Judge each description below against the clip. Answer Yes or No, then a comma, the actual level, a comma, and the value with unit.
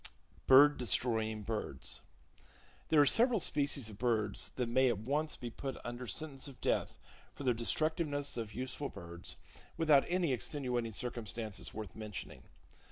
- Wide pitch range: No, average, 4.5 semitones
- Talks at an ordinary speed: Yes, average, 145 wpm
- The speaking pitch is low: Yes, low, 125 Hz